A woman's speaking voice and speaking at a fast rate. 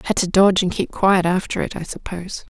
Yes: female; fast, 235 wpm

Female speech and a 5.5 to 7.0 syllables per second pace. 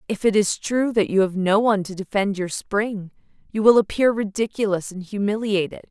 No: female; 5.3 syllables/s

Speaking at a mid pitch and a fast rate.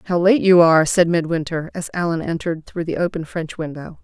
Yes: medium, 170 Hz; fast, 210 wpm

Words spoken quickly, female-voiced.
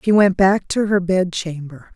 Yes: fast, 215 wpm; female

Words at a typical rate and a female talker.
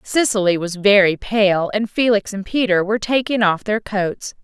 Yes: average, 175 wpm; female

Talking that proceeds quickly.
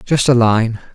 No: average, 190 wpm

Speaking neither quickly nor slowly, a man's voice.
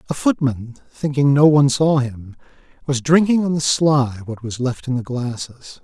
Yes: average, 185 wpm; male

